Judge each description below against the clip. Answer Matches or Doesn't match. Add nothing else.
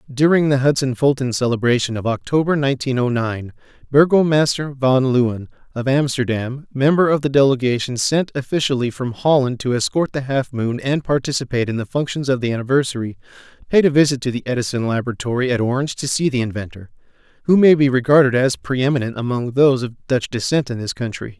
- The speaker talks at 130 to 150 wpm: Doesn't match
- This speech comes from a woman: Doesn't match